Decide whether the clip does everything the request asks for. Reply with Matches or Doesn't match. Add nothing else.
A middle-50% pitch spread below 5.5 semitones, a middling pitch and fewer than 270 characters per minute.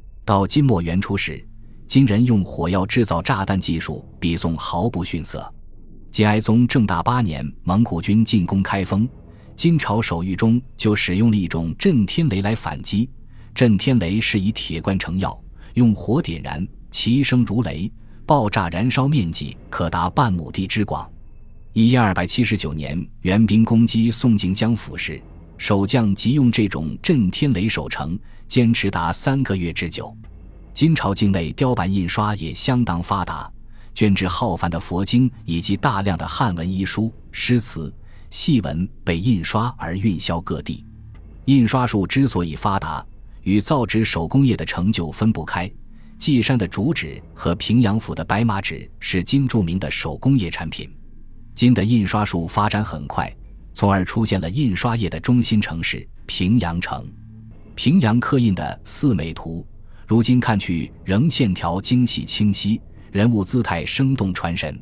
Doesn't match